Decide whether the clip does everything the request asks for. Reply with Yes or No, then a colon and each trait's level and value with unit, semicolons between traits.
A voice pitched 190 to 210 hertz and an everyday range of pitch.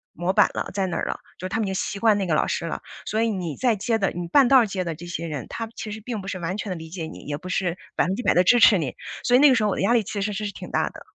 Yes: high, 195 Hz; average, 4.2 semitones